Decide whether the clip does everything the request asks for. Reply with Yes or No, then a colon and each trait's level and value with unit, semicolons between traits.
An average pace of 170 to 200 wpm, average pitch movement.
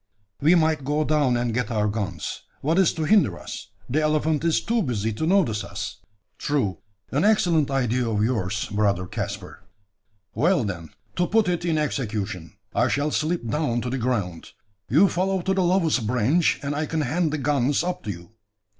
No: average, 185 wpm; wide, 7.0 semitones